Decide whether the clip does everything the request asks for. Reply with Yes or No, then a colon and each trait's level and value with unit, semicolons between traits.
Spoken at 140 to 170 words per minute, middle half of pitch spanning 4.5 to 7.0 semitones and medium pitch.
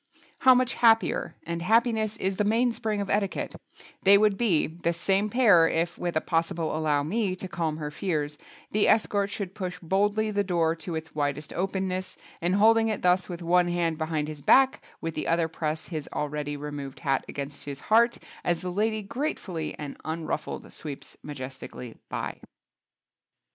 Yes: average, 165 wpm; average, 4.9 semitones; medium, 175 Hz